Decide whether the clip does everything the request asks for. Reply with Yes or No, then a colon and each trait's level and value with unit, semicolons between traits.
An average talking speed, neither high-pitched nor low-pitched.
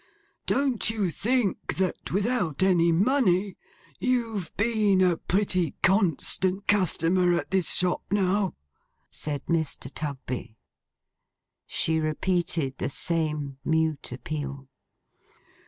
No: slow, 100 wpm; medium, 180 Hz